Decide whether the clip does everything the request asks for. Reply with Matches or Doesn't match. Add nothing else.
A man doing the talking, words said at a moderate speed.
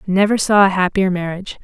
Doesn't match